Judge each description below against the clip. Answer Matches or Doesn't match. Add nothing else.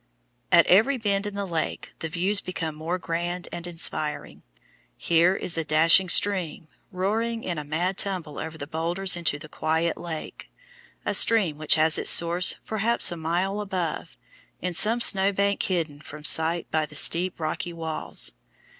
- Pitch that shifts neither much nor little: Matches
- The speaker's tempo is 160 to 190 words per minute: Matches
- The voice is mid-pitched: Matches